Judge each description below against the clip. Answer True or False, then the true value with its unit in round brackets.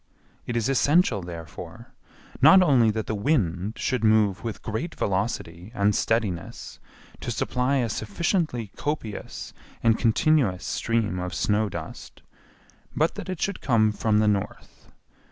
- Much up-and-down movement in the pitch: False (4.4 semitones)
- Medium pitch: False (110 Hz)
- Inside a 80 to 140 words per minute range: True (135 wpm)